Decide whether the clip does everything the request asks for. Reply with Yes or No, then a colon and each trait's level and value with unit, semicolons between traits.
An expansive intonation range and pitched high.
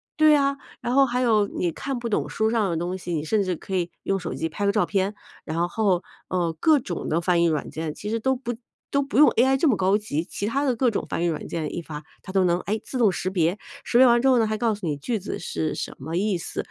Yes: wide, 5.7 semitones; high, 200 Hz